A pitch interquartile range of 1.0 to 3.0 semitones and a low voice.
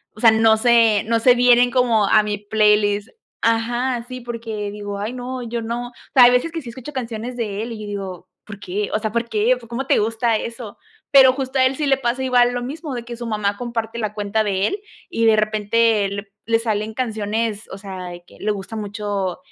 No: average, 2.7 semitones; high, 225 Hz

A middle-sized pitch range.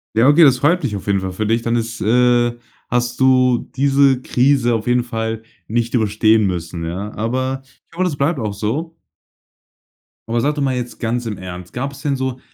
Yes: average, 3.3 semitones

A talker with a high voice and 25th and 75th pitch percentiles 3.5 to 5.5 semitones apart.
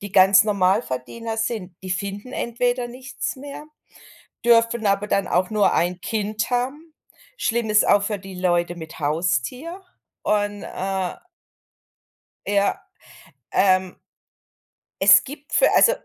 Yes: high, 205 Hz; average, 4.2 semitones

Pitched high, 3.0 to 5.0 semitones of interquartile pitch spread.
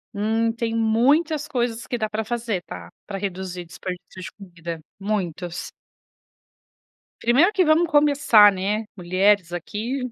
Yes: high, 215 Hz; average, 4.4 semitones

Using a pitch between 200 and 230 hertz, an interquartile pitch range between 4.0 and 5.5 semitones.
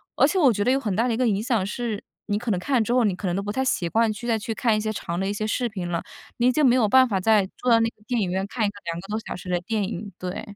No: high, 215 Hz; average, 3.6 semitones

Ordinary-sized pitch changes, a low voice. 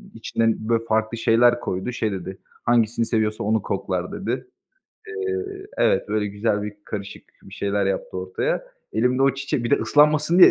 Yes: average, 3.4 semitones; low, 110 Hz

